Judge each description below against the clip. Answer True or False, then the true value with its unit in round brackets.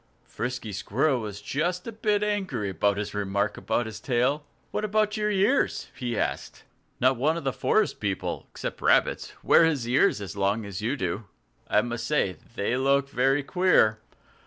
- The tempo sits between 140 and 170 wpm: False (180 wpm)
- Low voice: True (125 Hz)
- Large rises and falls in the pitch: True (7.6 semitones)